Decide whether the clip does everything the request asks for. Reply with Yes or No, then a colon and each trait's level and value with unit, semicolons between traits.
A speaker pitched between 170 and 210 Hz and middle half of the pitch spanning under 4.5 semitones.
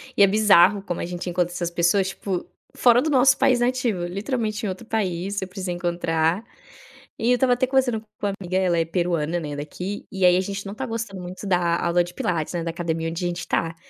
Yes: medium, 185 Hz; average, 3.7 semitones